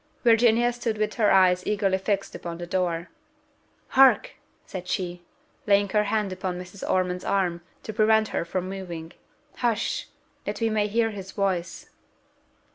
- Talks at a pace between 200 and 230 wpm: No, average, 150 wpm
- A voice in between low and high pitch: No, high, 195 Hz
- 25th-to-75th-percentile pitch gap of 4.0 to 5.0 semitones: No, average, 3.2 semitones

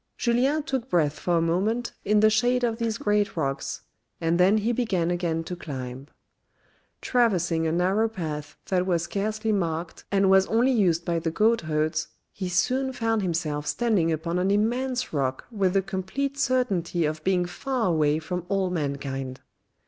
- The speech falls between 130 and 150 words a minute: No, average, 170 wpm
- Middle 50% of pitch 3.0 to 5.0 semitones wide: No, wide, 5.4 semitones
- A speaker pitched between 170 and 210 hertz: Yes, medium, 185 Hz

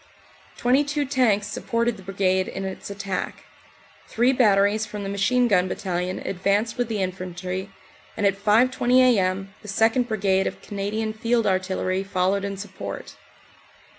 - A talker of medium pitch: No, high, 200 Hz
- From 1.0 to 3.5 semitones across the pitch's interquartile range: Yes, average, 3.2 semitones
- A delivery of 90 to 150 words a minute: Yes, average, 145 wpm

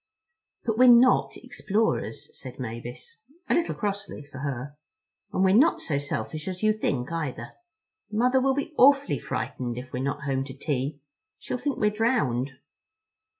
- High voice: No, medium, 155 Hz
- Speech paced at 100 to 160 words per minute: Yes, average, 155 wpm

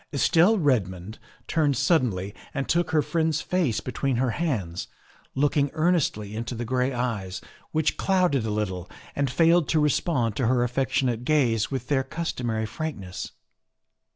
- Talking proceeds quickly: No, average, 145 wpm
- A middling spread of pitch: No, wide, 5.9 semitones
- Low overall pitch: Yes, low, 130 Hz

